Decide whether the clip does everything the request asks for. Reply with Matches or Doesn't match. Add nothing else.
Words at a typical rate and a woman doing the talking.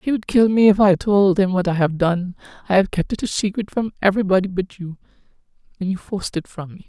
Doesn't match